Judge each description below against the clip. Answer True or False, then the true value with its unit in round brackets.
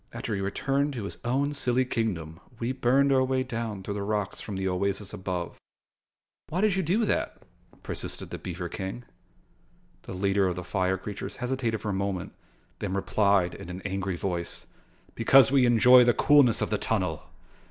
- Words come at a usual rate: True (180 wpm)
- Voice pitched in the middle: False (105 Hz)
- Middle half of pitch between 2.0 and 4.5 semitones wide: False (5.0 semitones)